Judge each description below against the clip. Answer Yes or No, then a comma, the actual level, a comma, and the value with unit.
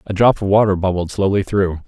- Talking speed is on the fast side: Yes, fast, 225 wpm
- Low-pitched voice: Yes, very low, 95 Hz